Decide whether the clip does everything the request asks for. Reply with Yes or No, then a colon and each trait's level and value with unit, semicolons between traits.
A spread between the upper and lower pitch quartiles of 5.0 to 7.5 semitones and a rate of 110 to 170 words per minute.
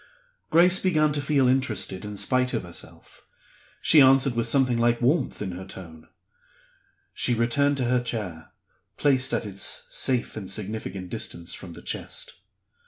Yes: wide, 5.6 semitones; average, 155 wpm